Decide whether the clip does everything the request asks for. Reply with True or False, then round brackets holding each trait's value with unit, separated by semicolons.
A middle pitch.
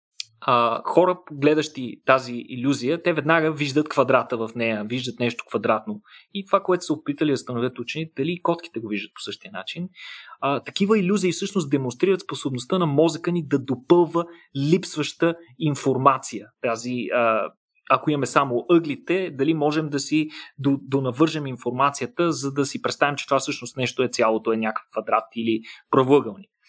True (145 Hz)